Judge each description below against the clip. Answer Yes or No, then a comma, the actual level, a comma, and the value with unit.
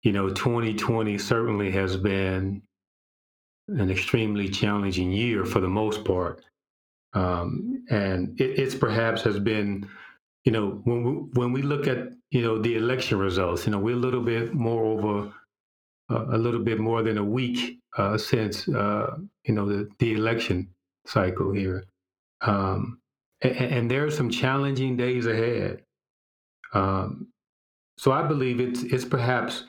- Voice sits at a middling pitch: No, low, 115 Hz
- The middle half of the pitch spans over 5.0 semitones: No, average, 4.0 semitones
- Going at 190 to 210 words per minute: No, average, 155 wpm